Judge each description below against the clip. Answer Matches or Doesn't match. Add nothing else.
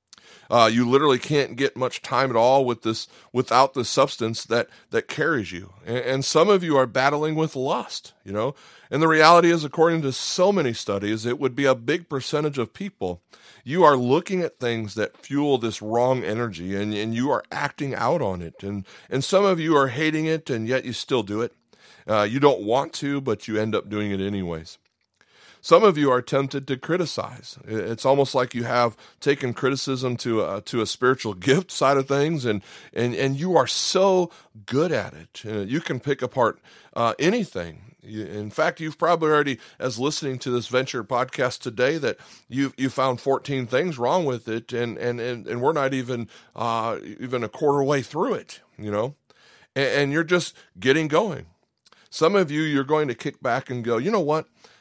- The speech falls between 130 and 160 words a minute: Doesn't match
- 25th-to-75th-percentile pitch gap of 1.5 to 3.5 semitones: Doesn't match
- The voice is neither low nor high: Doesn't match